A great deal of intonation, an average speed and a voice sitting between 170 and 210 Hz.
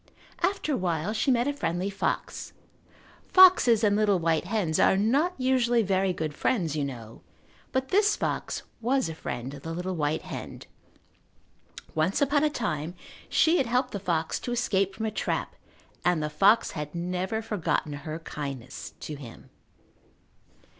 Yes: wide, 7.3 semitones; average, 160 wpm; high, 190 Hz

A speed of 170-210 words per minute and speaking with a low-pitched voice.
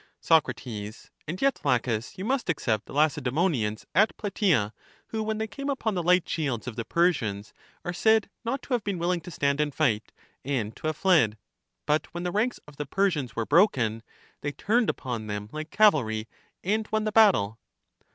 No: average, 190 wpm; medium, 155 Hz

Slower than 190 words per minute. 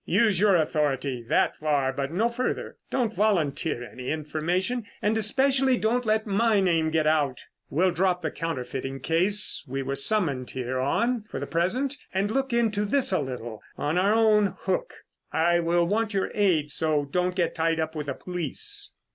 Yes: average, 175 wpm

